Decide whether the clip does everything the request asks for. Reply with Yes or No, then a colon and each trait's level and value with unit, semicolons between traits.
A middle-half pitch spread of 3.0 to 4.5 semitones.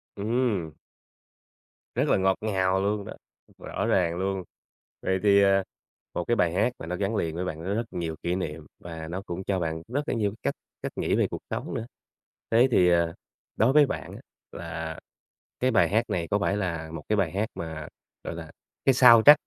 Yes: average, 4.1 semitones